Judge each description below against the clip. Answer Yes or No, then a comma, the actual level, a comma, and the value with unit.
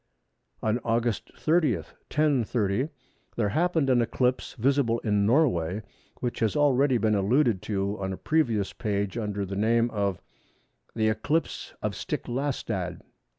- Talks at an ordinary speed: No, slow, 130 wpm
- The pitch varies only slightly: No, average, 4.7 semitones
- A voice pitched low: Yes, low, 115 Hz